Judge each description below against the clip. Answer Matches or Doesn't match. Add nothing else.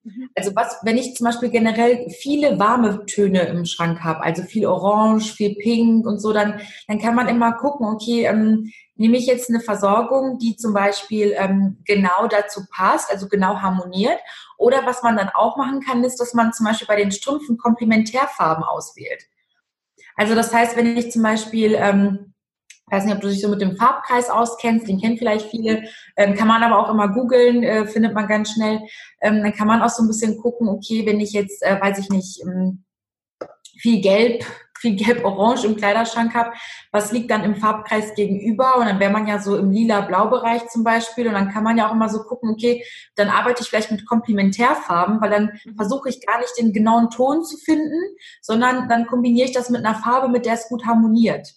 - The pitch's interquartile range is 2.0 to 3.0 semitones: Matches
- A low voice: Doesn't match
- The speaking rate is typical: Doesn't match